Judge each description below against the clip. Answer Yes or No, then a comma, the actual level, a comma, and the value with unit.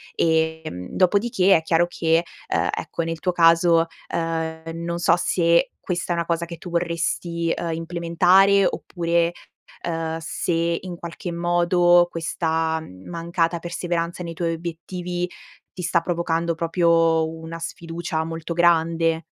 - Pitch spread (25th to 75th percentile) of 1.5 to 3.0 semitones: No, narrow, 1.0 semitones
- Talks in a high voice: No, medium, 170 Hz